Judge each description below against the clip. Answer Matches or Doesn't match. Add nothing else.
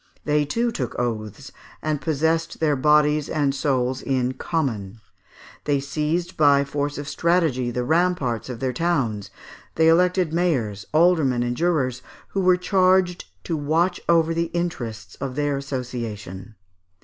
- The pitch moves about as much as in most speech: Matches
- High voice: Doesn't match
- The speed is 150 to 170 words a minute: Doesn't match